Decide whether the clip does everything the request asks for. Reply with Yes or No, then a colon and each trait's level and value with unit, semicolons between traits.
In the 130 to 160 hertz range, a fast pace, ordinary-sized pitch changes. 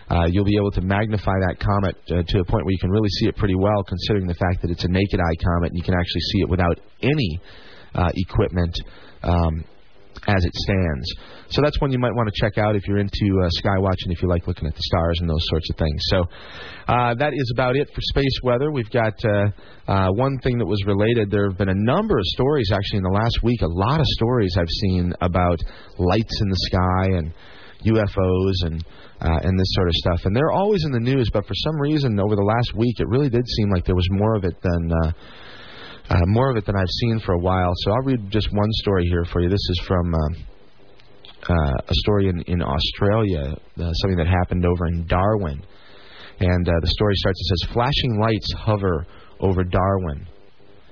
No: very low, 95 Hz; fast, 230 wpm; average, 3.4 semitones